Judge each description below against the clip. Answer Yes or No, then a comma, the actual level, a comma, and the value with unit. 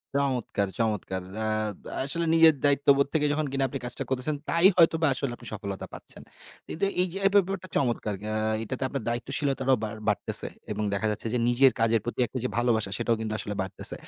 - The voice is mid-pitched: No, low, 130 Hz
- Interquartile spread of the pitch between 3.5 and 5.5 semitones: Yes, average, 4.6 semitones